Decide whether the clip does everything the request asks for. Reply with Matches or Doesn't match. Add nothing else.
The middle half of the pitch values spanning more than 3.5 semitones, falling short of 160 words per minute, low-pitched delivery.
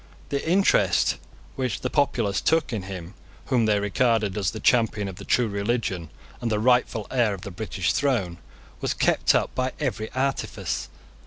Doesn't match